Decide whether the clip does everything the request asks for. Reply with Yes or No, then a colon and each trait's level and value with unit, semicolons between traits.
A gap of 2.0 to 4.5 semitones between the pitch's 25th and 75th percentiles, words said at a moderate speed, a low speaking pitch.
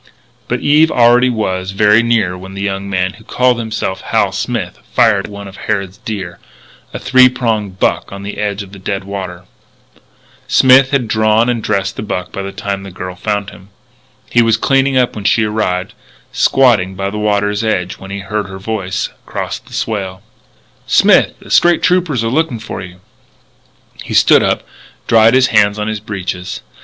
Yes: average, 3.0 semitones; average, 185 wpm; low, 105 Hz